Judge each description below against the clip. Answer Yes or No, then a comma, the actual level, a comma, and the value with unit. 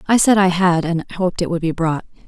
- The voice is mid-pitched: Yes, medium, 175 Hz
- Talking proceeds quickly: Yes, fast, 265 wpm